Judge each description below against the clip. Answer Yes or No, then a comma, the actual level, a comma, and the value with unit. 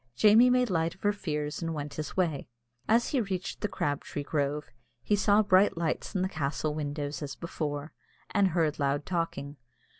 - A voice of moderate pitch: Yes, medium, 160 Hz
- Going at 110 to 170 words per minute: No, average, 180 wpm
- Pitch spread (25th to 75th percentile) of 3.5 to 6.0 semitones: Yes, average, 5.0 semitones